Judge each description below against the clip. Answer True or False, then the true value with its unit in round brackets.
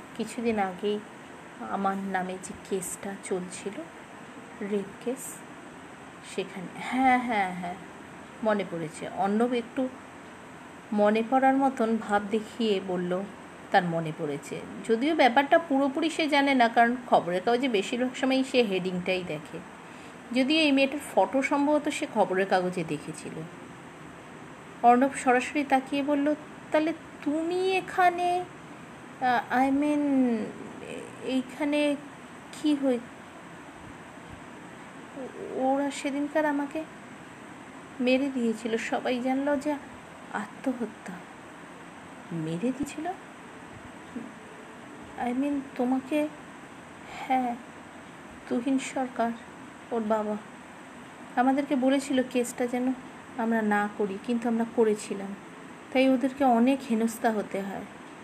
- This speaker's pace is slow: True (100 wpm)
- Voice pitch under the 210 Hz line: False (245 Hz)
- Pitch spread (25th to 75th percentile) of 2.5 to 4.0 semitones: False (4.5 semitones)